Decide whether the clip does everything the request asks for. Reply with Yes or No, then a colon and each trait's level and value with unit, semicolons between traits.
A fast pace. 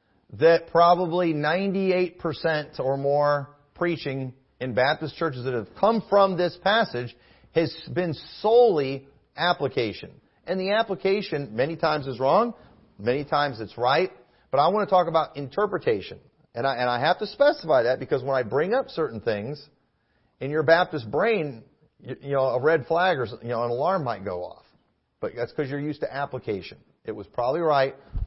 No: average, 170 wpm